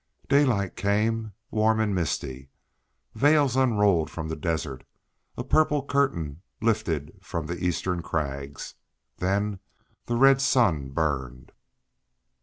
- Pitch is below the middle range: Yes, very low, 95 Hz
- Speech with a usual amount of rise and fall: No, wide, 6.6 semitones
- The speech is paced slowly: Yes, slow, 110 wpm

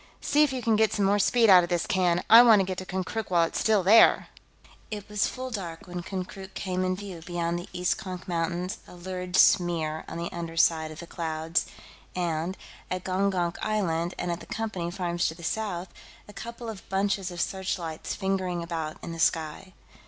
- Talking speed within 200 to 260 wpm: Yes, fast, 205 wpm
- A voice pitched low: No, medium, 180 Hz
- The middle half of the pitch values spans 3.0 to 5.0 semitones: No, narrow, 2.6 semitones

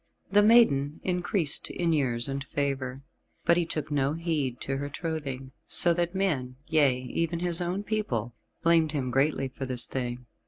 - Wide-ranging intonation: No, average, 4.3 semitones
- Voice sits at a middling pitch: Yes, medium, 145 Hz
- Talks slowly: No, average, 165 wpm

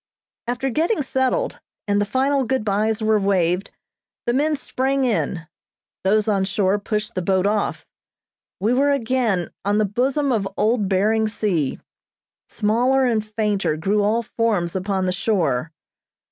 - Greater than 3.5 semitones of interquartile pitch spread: Yes, average, 4.1 semitones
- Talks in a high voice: Yes, high, 215 Hz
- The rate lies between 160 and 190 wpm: No, average, 145 wpm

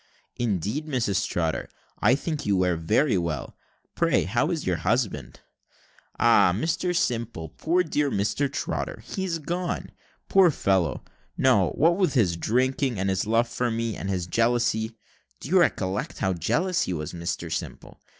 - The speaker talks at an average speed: Yes, average, 155 wpm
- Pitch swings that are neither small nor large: No, wide, 8.0 semitones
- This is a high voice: No, low, 115 Hz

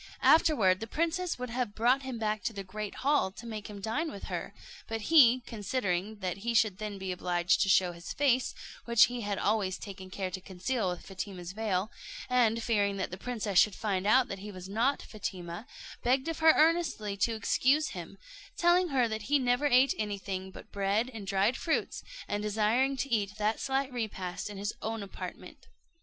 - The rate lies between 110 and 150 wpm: No, average, 195 wpm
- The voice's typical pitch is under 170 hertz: No, high, 215 Hz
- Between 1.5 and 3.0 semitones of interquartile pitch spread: No, average, 4.3 semitones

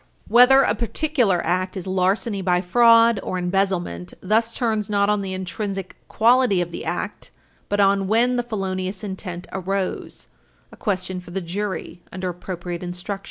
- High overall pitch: Yes, high, 195 Hz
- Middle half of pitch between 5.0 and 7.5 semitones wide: No, average, 3.0 semitones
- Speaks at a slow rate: No, average, 160 wpm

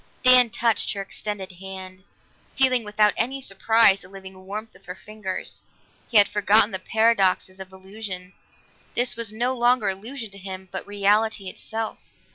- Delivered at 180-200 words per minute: No, average, 155 wpm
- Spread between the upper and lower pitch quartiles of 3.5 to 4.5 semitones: No, average, 3.0 semitones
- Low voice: No, high, 205 Hz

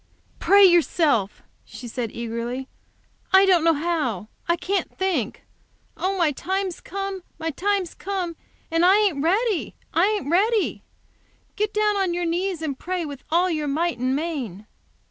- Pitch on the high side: Yes, very high, 340 Hz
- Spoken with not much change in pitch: No, average, 5.1 semitones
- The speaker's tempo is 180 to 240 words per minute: No, average, 155 wpm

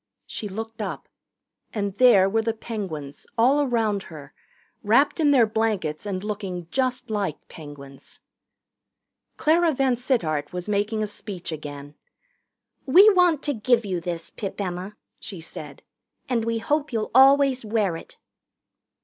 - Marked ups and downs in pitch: Yes, wide, 5.8 semitones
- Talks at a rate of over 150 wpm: No, average, 140 wpm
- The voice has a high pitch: Yes, high, 215 Hz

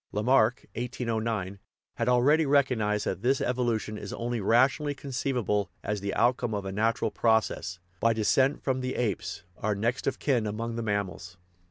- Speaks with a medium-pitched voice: No, low, 115 Hz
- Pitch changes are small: No, average, 3.3 semitones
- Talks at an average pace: Yes, average, 160 wpm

